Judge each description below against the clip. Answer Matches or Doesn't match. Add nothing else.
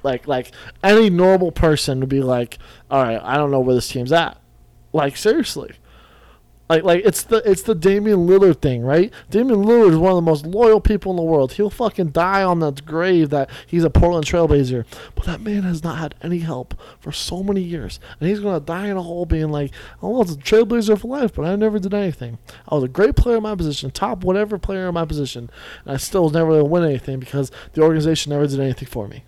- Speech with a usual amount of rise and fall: Doesn't match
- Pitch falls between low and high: Matches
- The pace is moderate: Doesn't match